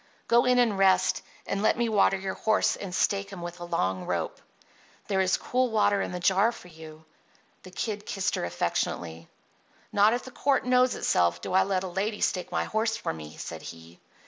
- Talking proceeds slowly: No, fast, 205 wpm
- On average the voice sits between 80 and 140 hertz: No, high, 195 Hz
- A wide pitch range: No, average, 4.0 semitones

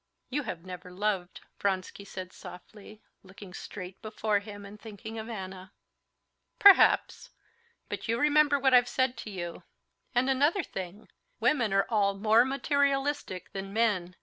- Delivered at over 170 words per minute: No, average, 145 wpm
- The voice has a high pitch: Yes, high, 210 Hz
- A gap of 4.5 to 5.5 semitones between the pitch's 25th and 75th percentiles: Yes, average, 4.9 semitones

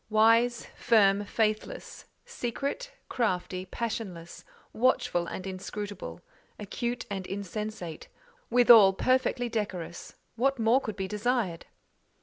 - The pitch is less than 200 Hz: No, high, 215 Hz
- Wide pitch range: No, average, 4.0 semitones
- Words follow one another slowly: Yes, slow, 90 wpm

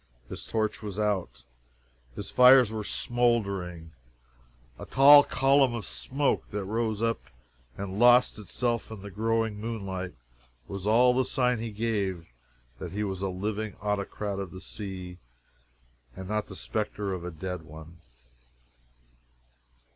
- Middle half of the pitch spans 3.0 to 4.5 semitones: Yes, average, 3.5 semitones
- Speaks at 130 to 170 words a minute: Yes, average, 140 wpm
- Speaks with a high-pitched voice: No, low, 105 Hz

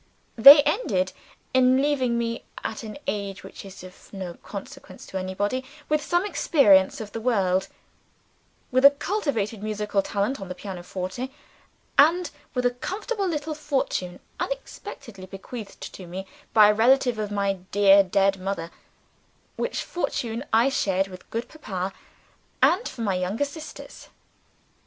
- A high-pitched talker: Yes, high, 215 Hz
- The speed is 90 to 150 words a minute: Yes, average, 140 wpm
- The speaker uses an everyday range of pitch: No, wide, 5.9 semitones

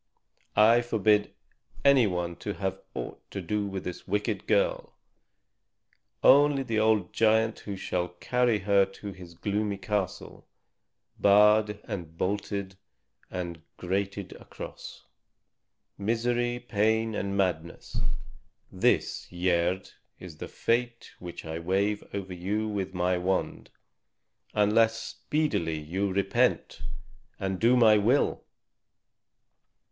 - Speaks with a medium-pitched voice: No, low, 100 Hz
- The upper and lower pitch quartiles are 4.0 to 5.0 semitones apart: No, average, 3.2 semitones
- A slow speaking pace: Yes, slow, 110 wpm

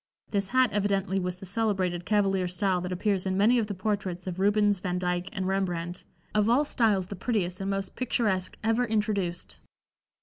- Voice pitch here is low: No, high, 195 Hz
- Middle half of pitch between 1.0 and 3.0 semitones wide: Yes, narrow, 2.5 semitones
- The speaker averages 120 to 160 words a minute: No, average, 175 wpm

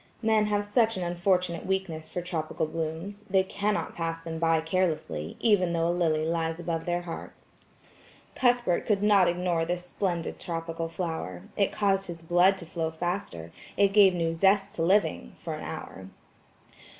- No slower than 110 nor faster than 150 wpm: No, average, 160 wpm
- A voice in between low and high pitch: Yes, medium, 175 Hz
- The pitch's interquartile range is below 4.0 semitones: Yes, average, 3.0 semitones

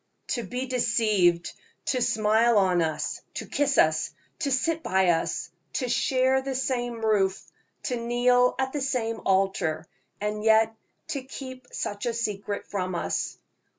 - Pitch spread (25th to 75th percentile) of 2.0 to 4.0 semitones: No, average, 4.7 semitones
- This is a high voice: Yes, high, 230 Hz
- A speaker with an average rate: Yes, average, 150 wpm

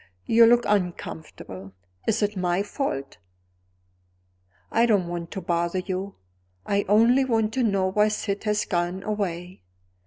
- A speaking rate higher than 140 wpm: No, slow, 135 wpm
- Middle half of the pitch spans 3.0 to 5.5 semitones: Yes, average, 3.4 semitones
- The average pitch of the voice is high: Yes, high, 200 Hz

